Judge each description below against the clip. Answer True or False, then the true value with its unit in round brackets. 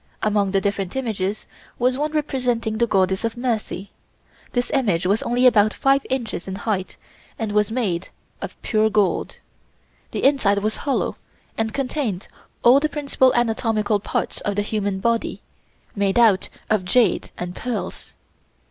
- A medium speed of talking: True (150 wpm)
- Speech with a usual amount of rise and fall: True (3.7 semitones)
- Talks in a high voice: True (220 Hz)